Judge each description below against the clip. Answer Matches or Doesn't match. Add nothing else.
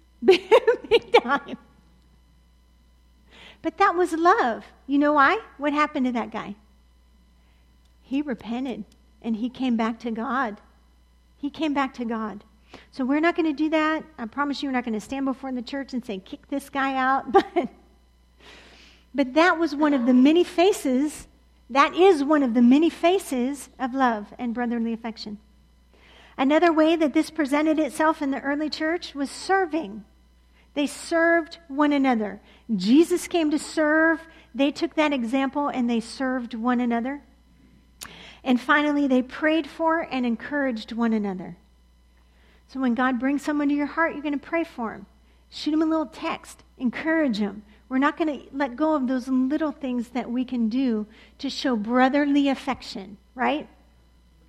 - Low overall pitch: Doesn't match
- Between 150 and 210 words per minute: Matches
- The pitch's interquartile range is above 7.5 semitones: Doesn't match